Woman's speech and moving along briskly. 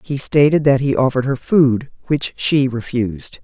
No: female; average, 175 wpm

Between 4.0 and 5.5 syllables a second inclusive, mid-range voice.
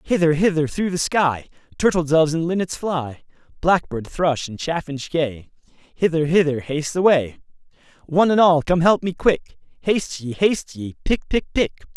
Yes: 4.9 syllables/s; medium, 160 Hz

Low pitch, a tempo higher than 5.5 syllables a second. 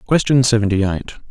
Yes: low, 115 Hz; 5.9 syllables/s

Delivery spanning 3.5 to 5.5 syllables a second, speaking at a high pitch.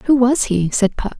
Yes: 4.9 syllables/s; high, 235 Hz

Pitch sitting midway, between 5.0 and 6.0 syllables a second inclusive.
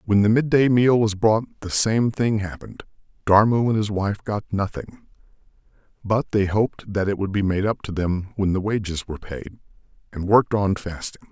No: low, 105 Hz; 5.3 syllables/s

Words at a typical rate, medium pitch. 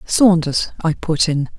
Yes: average, 150 wpm; medium, 170 Hz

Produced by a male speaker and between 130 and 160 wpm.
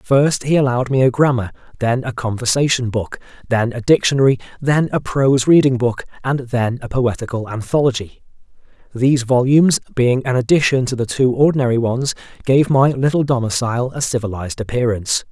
Yes: male; average, 155 wpm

